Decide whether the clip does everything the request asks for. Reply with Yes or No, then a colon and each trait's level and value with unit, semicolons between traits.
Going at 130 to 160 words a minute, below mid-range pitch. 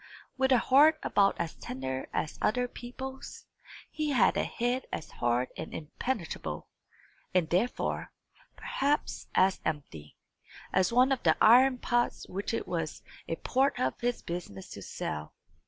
No: average, 145 wpm; high, 215 Hz